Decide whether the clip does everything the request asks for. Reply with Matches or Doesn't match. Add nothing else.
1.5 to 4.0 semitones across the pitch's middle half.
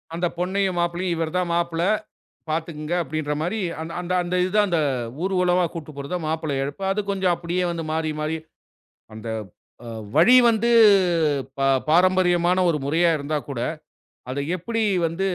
Matches